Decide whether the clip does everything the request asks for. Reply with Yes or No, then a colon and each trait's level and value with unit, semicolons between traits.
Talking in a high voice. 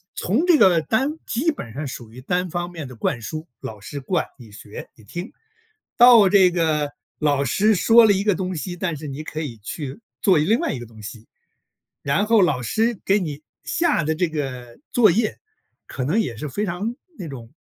No: medium, 165 Hz